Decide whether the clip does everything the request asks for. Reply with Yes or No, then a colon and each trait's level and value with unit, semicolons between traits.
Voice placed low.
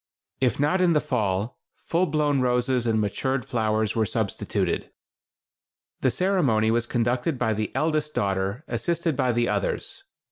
Yes: low, 125 Hz